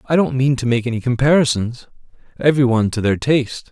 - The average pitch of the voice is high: No, low, 125 Hz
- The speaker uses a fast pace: No, average, 195 wpm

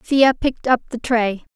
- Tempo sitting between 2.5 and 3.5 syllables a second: No, 4.9 syllables/s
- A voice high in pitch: Yes, high, 245 Hz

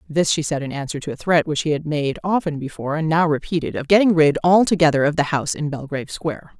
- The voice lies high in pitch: No, medium, 155 Hz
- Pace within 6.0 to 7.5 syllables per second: Yes, 6.5 syllables/s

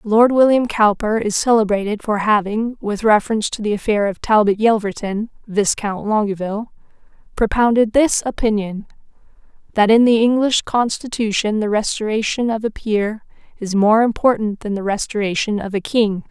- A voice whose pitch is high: Yes, high, 215 Hz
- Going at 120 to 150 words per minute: Yes, average, 145 wpm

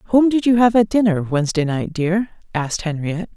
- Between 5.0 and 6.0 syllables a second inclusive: Yes, 5.6 syllables/s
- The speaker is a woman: Yes, female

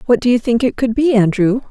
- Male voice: No, female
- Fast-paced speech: Yes, fast, 280 wpm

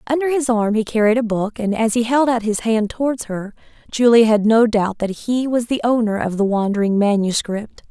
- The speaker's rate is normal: No, fast, 220 wpm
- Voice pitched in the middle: No, high, 225 Hz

